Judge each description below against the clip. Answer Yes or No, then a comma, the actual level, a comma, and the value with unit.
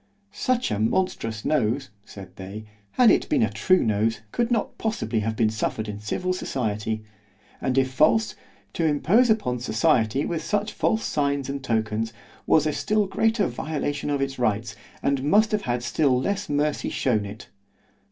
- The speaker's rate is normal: Yes, average, 160 wpm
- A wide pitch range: Yes, wide, 8.8 semitones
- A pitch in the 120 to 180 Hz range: Yes, low, 135 Hz